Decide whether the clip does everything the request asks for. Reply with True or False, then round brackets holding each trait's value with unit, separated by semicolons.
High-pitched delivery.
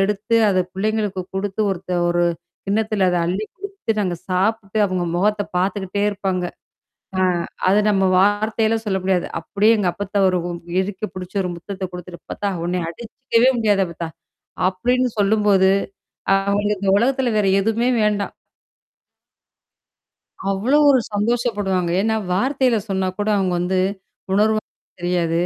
True (200 Hz)